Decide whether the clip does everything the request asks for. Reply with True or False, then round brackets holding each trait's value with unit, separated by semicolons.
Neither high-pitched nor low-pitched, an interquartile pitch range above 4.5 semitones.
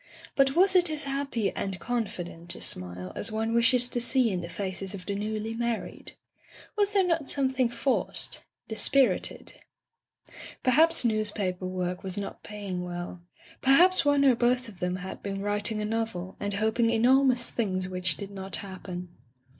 False (220 Hz; 5.4 semitones)